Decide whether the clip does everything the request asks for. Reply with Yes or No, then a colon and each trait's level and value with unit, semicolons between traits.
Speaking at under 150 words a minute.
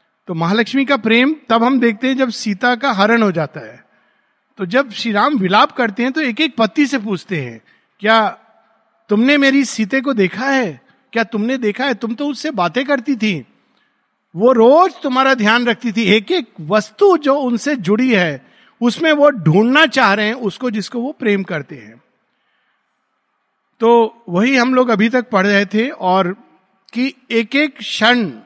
No: average, 175 wpm